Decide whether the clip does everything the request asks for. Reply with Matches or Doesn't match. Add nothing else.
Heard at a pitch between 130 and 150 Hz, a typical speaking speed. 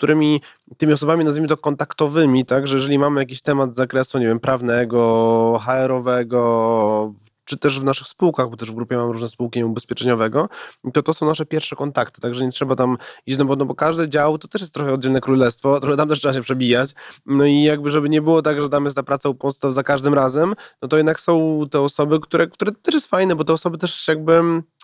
Doesn't match